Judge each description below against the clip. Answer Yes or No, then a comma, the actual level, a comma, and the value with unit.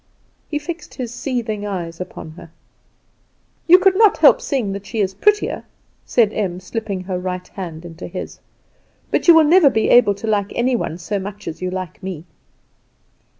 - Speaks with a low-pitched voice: No, high, 205 Hz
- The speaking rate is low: No, average, 180 wpm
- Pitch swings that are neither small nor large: No, wide, 5.7 semitones